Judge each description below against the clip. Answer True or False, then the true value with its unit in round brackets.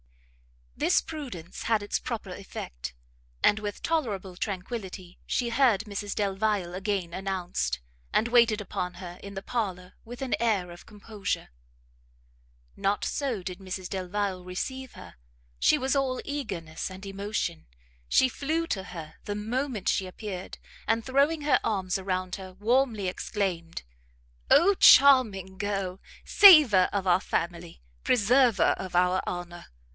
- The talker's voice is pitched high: True (200 Hz)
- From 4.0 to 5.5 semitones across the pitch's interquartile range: True (4.4 semitones)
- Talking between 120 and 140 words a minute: True (135 wpm)